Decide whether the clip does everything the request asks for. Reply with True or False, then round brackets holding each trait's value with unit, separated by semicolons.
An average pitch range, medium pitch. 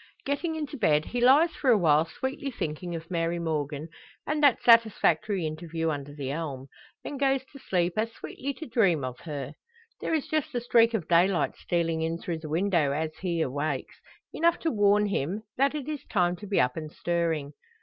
False (7.5 semitones; 175 Hz)